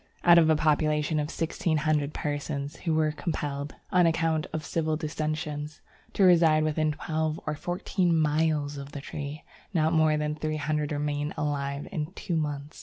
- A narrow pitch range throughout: Yes, narrow, 1.3 semitones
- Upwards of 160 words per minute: Yes, average, 170 wpm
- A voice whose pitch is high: No, medium, 155 Hz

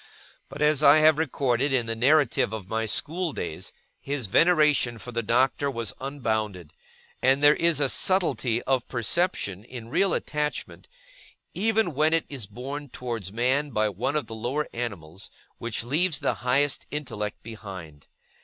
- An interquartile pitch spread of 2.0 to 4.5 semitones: No, average, 4.9 semitones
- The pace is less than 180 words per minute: Yes, average, 155 wpm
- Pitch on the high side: No, low, 130 Hz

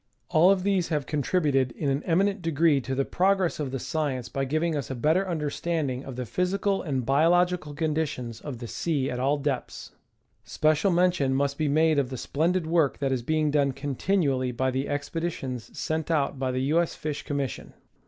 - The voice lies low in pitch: No, medium, 150 Hz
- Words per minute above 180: Yes, average, 190 wpm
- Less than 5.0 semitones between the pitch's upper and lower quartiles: Yes, average, 3.8 semitones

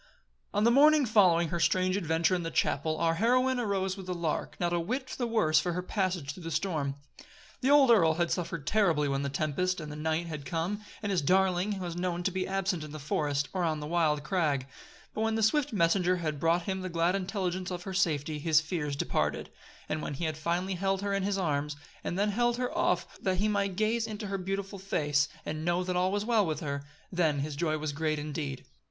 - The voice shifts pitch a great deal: No, average, 4.0 semitones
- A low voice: No, medium, 180 Hz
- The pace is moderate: No, fast, 230 wpm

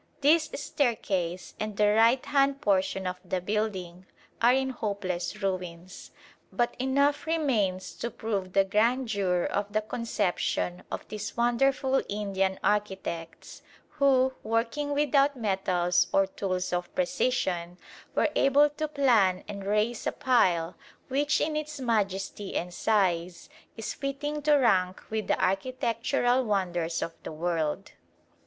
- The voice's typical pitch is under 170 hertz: No, high, 210 Hz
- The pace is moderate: No, slow, 130 wpm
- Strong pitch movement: Yes, wide, 6.1 semitones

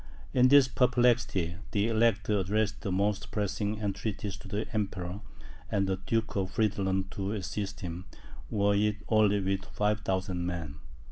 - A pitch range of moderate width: No, narrow, 2.2 semitones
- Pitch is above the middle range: No, low, 100 Hz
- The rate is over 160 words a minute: No, average, 145 wpm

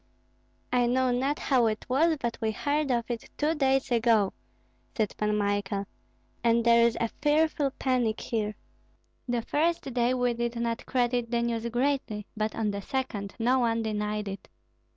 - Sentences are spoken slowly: No, average, 170 wpm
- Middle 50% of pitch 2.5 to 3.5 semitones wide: Yes, average, 2.9 semitones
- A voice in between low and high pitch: No, high, 235 Hz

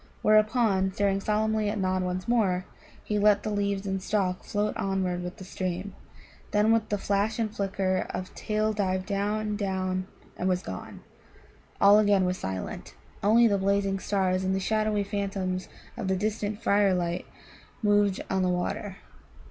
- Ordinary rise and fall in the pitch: No, narrow, 2.0 semitones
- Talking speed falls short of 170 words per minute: Yes, average, 160 wpm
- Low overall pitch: No, high, 200 Hz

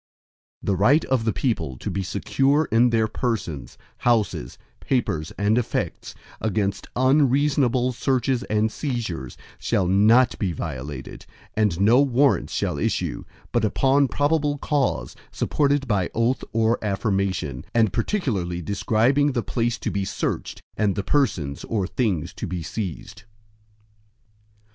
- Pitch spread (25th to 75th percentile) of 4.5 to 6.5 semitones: Yes, average, 5.2 semitones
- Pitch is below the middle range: Yes, low, 110 Hz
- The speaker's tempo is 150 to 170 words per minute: No, slow, 135 wpm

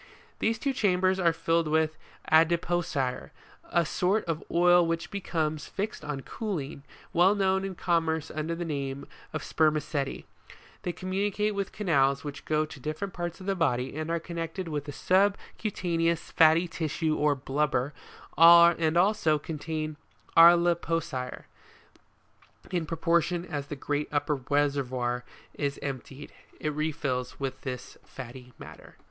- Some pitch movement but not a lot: Yes, average, 3.2 semitones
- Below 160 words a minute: Yes, average, 140 wpm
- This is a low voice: No, medium, 160 Hz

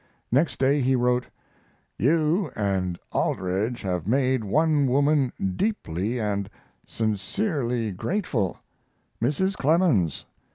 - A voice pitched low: Yes, low, 125 Hz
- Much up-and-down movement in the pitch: Yes, wide, 6.8 semitones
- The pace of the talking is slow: Yes, slow, 95 wpm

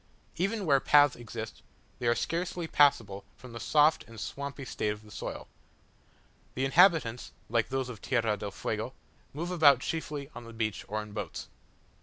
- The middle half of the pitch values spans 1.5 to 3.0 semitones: No, average, 4.9 semitones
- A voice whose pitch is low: Yes, low, 130 Hz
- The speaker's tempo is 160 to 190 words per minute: Yes, average, 170 wpm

